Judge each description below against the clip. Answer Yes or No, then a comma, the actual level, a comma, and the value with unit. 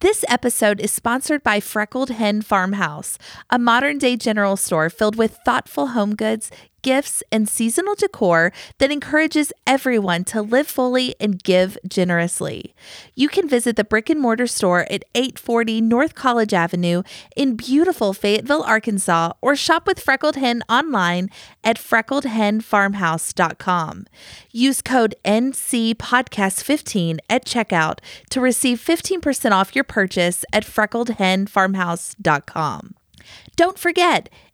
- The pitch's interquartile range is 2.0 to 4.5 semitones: No, average, 5.0 semitones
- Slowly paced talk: Yes, slow, 125 wpm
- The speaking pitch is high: Yes, high, 230 Hz